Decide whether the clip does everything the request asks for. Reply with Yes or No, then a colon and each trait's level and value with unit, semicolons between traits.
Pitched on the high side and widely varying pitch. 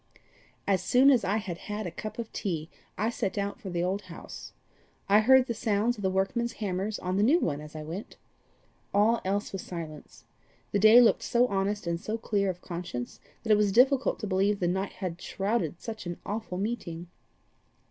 No: high, 200 Hz; average, 3.5 semitones